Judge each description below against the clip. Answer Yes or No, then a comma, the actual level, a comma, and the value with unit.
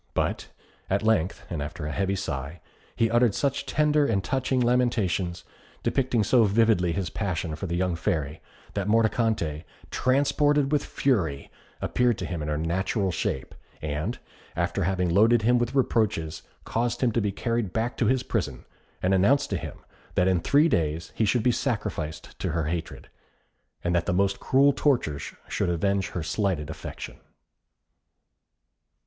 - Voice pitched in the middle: No, low, 100 Hz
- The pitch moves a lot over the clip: Yes, wide, 6.1 semitones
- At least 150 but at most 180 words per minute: Yes, average, 160 wpm